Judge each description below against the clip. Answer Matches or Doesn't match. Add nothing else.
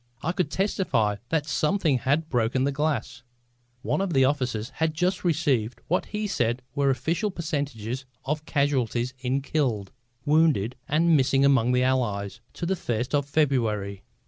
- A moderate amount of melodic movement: Matches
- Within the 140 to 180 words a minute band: Matches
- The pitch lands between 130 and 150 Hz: Matches